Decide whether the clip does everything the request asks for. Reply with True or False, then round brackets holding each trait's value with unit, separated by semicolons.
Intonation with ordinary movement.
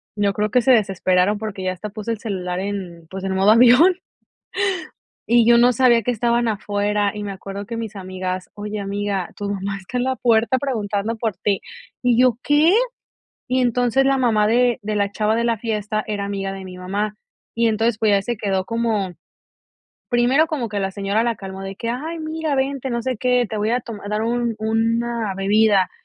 True (3.1 semitones)